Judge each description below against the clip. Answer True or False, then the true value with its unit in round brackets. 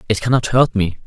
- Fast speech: True (225 wpm)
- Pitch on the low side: True (110 Hz)